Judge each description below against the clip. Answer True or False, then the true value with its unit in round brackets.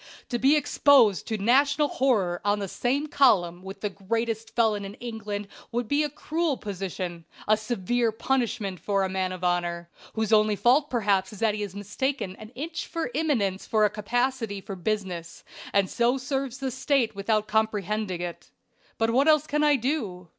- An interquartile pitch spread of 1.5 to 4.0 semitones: False (5.0 semitones)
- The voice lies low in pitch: False (220 Hz)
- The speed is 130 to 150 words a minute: False (180 wpm)